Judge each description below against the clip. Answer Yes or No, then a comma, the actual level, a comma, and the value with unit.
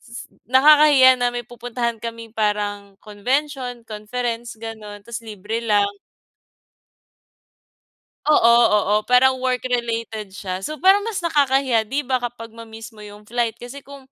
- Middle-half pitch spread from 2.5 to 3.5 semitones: Yes, average, 3.0 semitones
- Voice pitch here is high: Yes, high, 235 Hz